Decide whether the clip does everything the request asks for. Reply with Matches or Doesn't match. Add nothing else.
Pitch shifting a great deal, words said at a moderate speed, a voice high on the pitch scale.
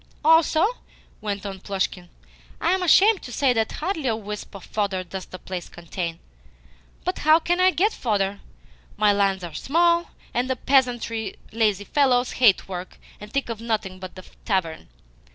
Matches